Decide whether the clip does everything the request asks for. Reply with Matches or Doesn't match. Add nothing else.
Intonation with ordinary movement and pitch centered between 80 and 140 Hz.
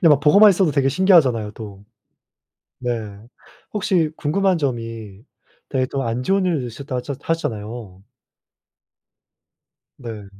Doesn't match